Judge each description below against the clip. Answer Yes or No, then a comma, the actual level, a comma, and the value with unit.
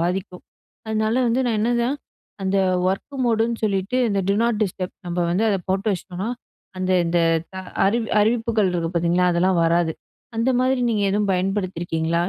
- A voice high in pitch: Yes, high, 195 Hz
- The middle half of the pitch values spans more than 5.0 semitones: No, average, 3.8 semitones